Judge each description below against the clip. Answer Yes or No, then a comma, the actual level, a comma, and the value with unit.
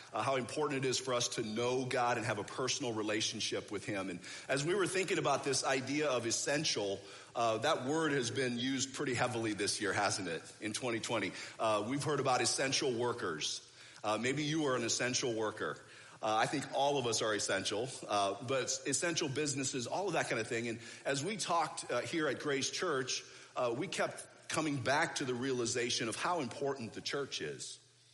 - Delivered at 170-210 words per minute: Yes, fast, 205 wpm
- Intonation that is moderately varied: Yes, average, 3.4 semitones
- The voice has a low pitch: Yes, low, 125 Hz